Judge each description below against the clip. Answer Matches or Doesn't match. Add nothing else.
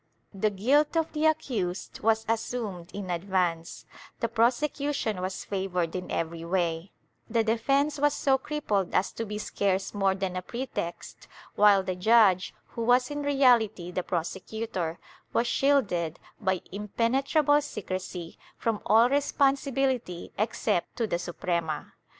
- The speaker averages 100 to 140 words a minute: Matches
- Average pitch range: Doesn't match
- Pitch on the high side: Matches